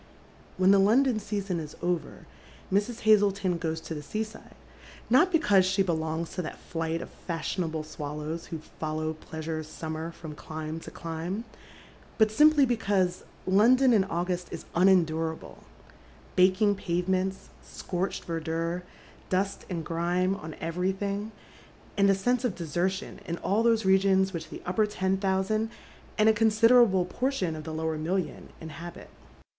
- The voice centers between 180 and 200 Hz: Yes, medium, 185 Hz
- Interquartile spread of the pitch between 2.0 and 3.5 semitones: No, average, 3.9 semitones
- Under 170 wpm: Yes, average, 150 wpm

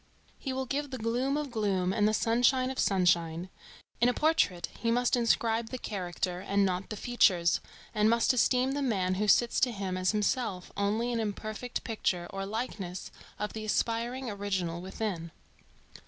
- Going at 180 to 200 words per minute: No, average, 170 wpm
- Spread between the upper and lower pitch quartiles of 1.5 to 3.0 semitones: No, average, 4.5 semitones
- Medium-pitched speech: No, high, 215 Hz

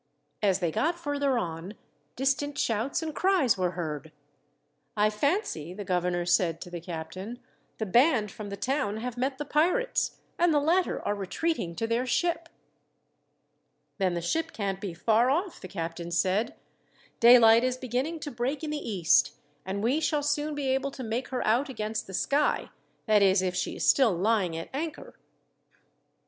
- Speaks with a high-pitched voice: Yes, high, 230 Hz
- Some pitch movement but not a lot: No, wide, 7.4 semitones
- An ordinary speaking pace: Yes, average, 175 wpm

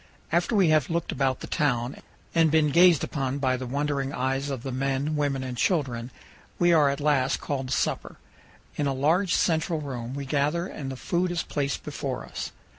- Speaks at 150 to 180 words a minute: No, average, 195 wpm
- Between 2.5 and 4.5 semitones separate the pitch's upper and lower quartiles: Yes, average, 3.2 semitones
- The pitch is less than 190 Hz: Yes, medium, 140 Hz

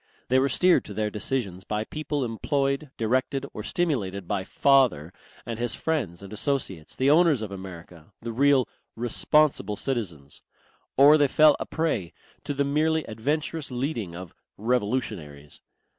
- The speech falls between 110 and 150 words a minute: Yes, average, 145 wpm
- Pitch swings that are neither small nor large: No, wide, 6.2 semitones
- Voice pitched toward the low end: Yes, low, 120 Hz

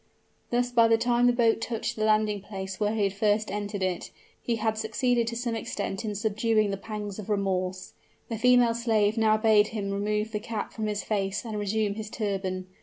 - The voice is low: No, high, 215 Hz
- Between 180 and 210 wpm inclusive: Yes, fast, 205 wpm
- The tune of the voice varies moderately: No, narrow, 1.9 semitones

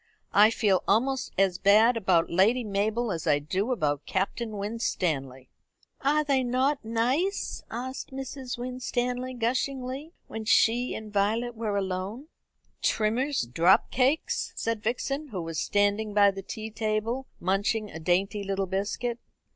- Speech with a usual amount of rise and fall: Yes, average, 4.2 semitones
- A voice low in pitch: No, high, 220 Hz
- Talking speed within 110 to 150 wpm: Yes, average, 140 wpm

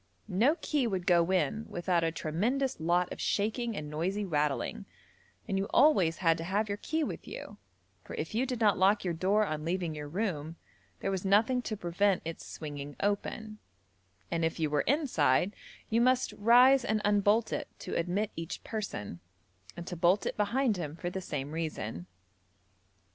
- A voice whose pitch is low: No, high, 190 Hz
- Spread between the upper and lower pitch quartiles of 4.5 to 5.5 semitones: Yes, average, 4.9 semitones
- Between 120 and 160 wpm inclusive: No, average, 180 wpm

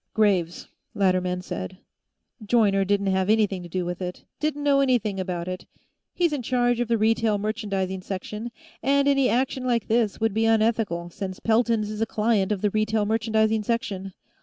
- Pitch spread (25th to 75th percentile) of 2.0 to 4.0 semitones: Yes, average, 3.3 semitones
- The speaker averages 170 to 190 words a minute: Yes, average, 175 wpm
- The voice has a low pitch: No, high, 215 Hz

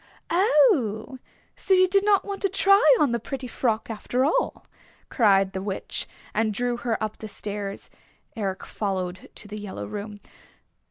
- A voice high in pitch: Yes, high, 220 Hz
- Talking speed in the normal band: Yes, average, 155 wpm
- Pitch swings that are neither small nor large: No, wide, 6.2 semitones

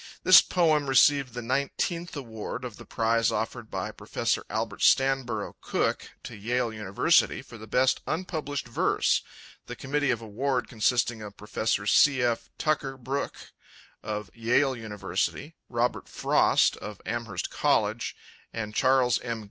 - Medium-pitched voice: No, low, 120 Hz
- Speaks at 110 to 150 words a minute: Yes, average, 140 wpm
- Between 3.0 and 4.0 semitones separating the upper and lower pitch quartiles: Yes, average, 3.5 semitones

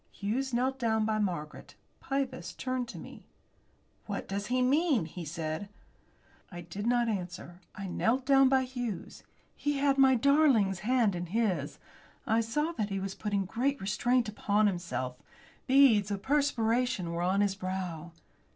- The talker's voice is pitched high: Yes, high, 220 Hz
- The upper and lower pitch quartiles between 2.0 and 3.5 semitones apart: No, average, 5.3 semitones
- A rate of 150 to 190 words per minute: Yes, average, 155 wpm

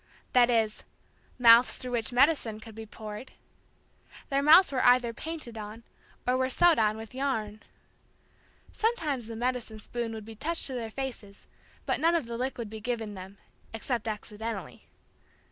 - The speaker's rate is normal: Yes, average, 160 wpm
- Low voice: No, high, 235 Hz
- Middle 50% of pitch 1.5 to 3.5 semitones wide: Yes, average, 3.1 semitones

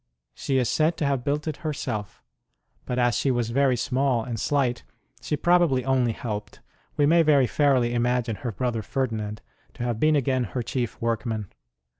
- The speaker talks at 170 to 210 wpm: Yes, average, 175 wpm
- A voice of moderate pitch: No, low, 125 Hz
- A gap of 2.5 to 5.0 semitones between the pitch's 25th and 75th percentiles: Yes, average, 3.1 semitones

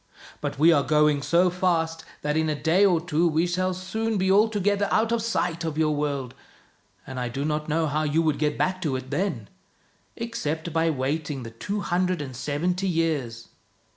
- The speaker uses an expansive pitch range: No, average, 3.8 semitones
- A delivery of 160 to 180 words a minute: No, average, 195 wpm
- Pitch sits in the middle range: Yes, medium, 160 Hz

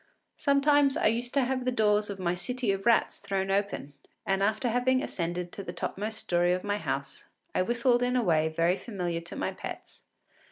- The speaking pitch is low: No, high, 205 Hz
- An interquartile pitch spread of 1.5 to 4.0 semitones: No, average, 5.3 semitones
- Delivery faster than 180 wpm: Yes, average, 200 wpm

